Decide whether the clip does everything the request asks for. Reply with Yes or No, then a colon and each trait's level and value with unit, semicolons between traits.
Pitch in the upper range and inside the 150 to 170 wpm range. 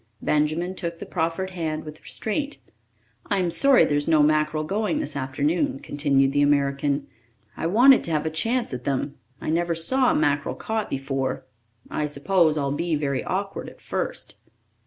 No: medium, 155 Hz; average, 160 wpm